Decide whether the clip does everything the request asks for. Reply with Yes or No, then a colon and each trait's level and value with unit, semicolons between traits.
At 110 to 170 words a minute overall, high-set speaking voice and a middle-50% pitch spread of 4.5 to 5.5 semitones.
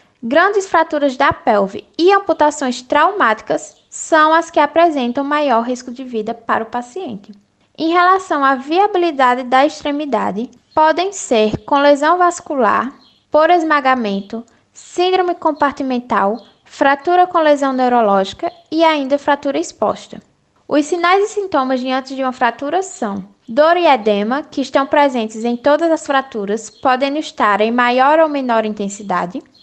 Yes: average, 135 wpm; very high, 280 Hz; average, 4.8 semitones